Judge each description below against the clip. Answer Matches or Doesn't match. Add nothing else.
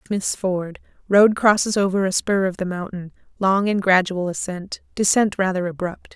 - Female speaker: Matches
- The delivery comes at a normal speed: Matches